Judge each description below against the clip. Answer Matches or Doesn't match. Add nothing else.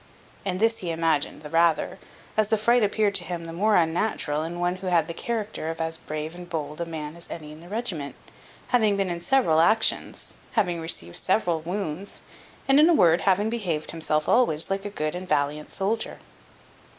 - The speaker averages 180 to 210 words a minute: Matches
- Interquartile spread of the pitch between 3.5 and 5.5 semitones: Matches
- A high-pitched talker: Doesn't match